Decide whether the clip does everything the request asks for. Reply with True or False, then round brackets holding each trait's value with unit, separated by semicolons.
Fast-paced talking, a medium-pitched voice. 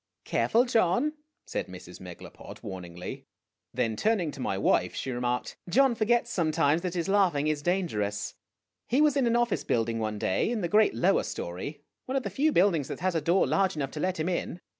True (210 wpm; 170 Hz)